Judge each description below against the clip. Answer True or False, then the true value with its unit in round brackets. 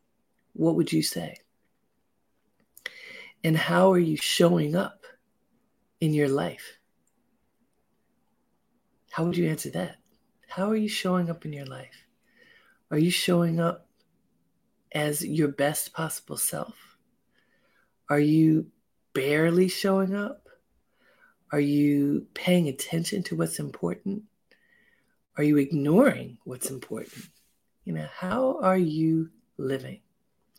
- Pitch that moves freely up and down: False (4.3 semitones)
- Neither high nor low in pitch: True (170 Hz)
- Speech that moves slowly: True (115 wpm)